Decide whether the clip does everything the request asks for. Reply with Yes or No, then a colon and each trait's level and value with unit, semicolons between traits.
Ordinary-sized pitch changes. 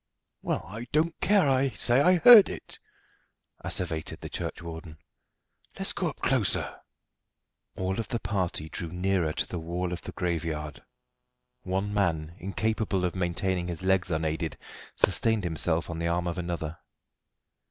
Yes: average, 3.6 semitones